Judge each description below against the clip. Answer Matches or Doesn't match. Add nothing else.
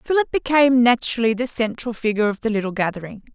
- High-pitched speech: Matches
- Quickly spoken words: Doesn't match